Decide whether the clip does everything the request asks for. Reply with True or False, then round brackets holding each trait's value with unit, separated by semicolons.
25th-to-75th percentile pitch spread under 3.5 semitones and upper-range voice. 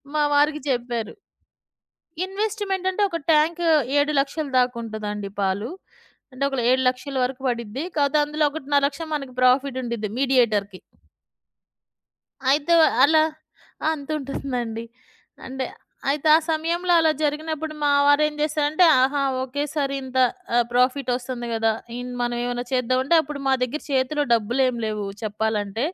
False (3.8 semitones; 270 Hz)